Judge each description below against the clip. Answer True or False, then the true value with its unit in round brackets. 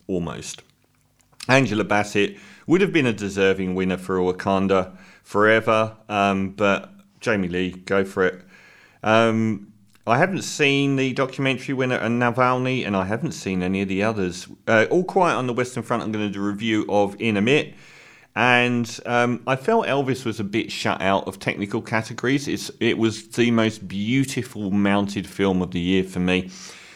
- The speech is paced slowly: False (175 wpm)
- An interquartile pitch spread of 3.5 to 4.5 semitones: True (4.1 semitones)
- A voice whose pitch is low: True (110 Hz)